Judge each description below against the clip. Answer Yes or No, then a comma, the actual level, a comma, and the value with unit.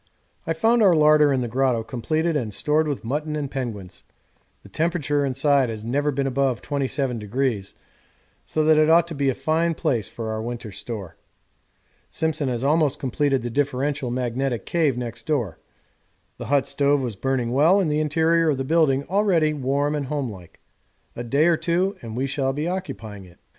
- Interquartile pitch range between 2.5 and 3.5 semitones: No, average, 4.1 semitones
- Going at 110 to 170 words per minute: No, average, 180 wpm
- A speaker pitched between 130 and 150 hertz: Yes, medium, 140 Hz